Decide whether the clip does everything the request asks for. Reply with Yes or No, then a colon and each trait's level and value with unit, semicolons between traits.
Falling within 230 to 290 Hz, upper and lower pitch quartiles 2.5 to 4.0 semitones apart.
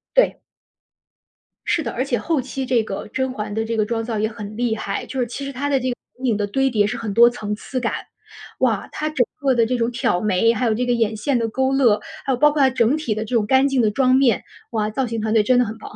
Yes: high, 235 Hz; average, 3.3 semitones